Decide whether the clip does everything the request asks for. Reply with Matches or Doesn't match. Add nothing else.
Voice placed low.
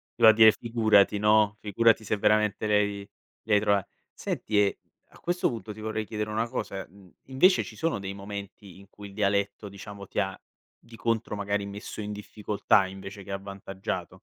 Matches